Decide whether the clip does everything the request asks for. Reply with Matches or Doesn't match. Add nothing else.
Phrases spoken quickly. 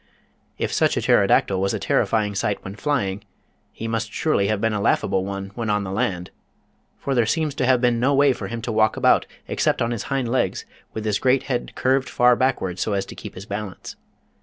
Matches